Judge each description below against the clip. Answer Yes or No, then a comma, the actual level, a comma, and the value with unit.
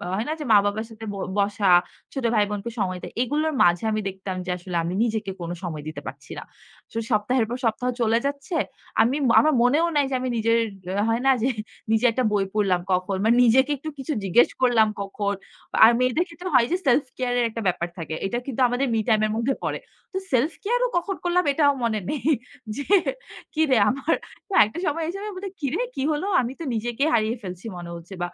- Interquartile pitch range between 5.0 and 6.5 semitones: Yes, average, 5.3 semitones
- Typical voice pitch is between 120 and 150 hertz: No, high, 235 Hz